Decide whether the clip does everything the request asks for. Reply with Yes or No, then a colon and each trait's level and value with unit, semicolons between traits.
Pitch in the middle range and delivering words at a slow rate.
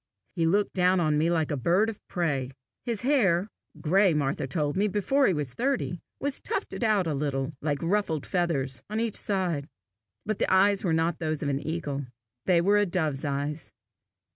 No: medium, 170 Hz; average, 190 wpm